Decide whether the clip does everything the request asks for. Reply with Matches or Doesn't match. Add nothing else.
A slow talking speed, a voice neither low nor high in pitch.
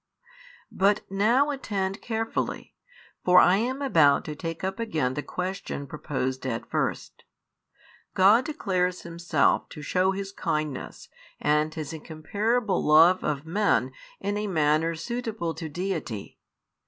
Matches